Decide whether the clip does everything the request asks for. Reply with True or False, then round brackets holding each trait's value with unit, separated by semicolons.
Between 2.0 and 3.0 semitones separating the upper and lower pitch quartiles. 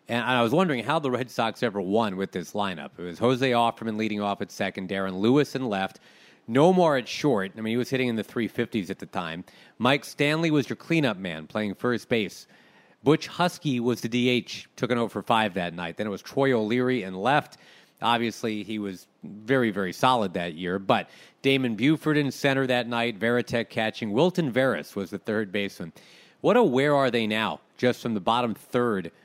False (4.0 semitones)